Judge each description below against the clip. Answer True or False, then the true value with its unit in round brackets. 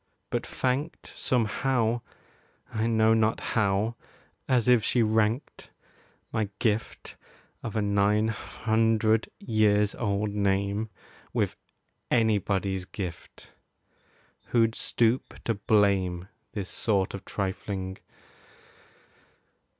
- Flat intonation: True (2.1 semitones)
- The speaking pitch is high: False (110 Hz)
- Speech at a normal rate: False (95 wpm)